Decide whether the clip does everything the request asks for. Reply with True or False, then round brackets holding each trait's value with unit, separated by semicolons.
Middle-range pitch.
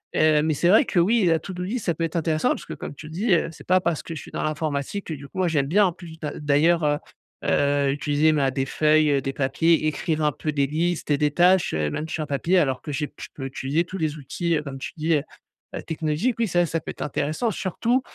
True (155 Hz)